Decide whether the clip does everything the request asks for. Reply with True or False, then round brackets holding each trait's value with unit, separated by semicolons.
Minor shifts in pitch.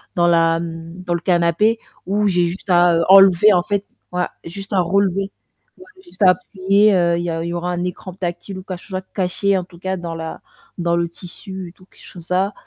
True (2.1 semitones)